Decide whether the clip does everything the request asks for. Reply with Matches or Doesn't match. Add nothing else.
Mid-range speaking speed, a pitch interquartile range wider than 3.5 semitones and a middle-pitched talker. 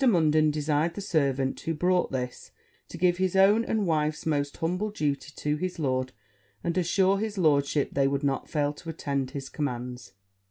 Matches